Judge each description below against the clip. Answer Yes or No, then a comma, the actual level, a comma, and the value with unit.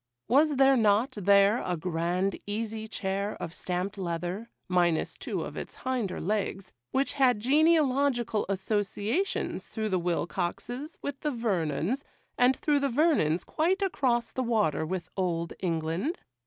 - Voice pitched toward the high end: Yes, high, 215 Hz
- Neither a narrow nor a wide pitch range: No, wide, 6.5 semitones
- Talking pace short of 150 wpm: Yes, average, 140 wpm